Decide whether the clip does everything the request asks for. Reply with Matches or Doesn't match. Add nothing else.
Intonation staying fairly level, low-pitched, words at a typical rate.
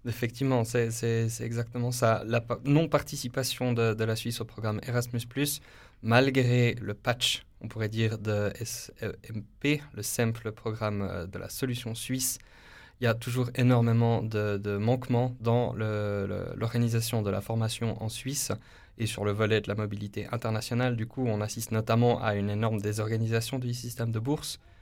Matches